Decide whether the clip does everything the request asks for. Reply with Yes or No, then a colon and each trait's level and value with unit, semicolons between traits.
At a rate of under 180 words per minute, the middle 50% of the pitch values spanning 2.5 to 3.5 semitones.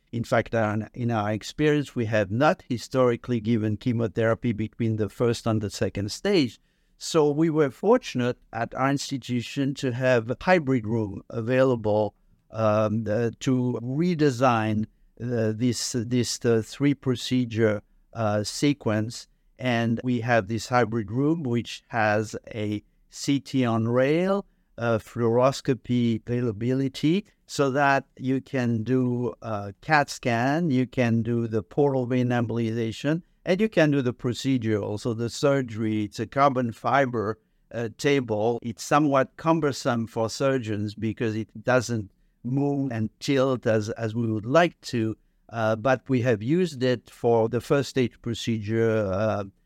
Yes: average, 140 wpm; average, 3.2 semitones